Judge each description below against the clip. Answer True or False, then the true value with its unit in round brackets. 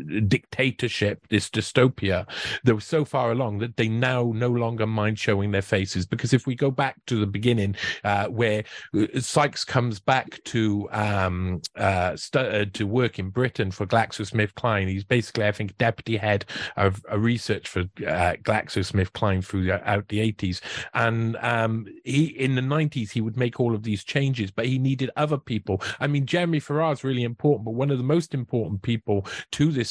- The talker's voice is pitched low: True (115 Hz)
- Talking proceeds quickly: False (185 wpm)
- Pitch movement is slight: False (3.8 semitones)